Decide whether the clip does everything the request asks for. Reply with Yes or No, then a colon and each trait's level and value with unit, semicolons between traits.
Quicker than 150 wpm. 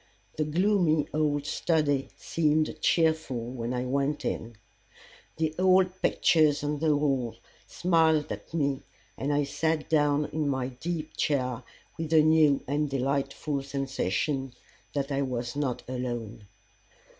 No: slow, 135 wpm